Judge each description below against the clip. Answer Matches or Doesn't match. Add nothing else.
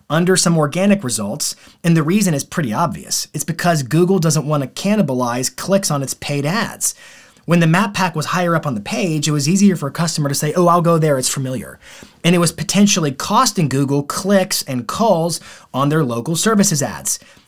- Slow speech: Doesn't match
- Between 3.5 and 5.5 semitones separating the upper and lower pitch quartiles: Matches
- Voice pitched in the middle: Matches